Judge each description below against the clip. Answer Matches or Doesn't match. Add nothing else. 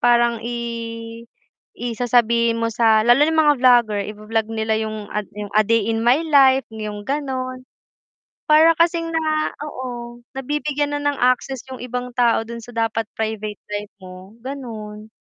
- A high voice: Matches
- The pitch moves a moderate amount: Matches